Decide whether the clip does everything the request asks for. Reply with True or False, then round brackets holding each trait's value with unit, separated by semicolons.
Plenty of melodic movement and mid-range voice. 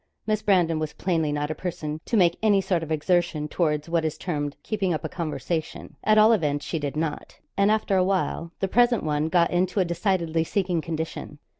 False (3.5 semitones; 170 Hz)